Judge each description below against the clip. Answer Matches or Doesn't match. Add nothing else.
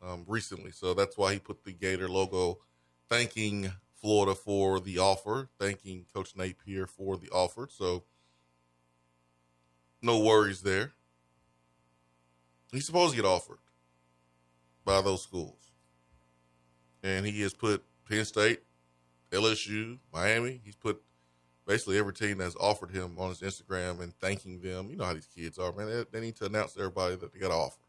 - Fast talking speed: Doesn't match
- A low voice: Matches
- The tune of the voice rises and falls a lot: Matches